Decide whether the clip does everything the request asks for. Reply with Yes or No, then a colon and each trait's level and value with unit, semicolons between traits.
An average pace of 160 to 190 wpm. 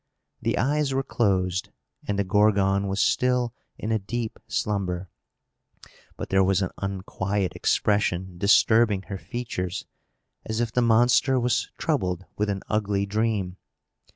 No: slow, 135 wpm